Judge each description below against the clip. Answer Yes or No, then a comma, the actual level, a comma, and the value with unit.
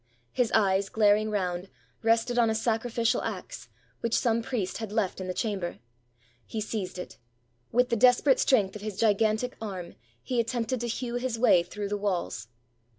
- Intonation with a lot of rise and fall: No, average, 3.1 semitones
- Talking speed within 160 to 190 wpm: Yes, average, 170 wpm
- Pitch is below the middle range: No, high, 220 Hz